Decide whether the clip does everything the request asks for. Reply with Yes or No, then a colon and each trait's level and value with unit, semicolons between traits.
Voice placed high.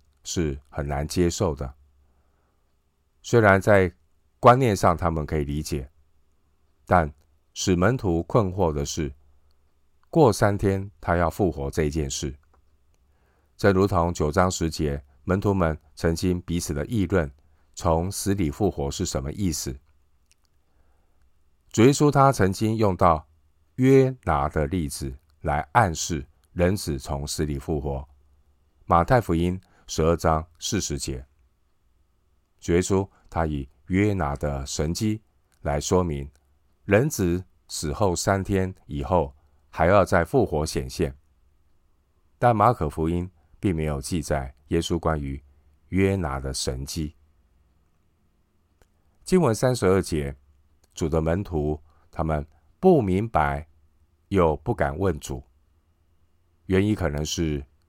No: very low, 80 Hz